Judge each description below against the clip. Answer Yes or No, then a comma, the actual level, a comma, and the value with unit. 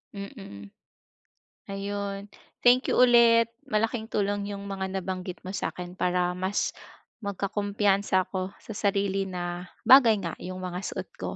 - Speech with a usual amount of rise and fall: No, narrow, 1.9 semitones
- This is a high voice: Yes, high, 195 Hz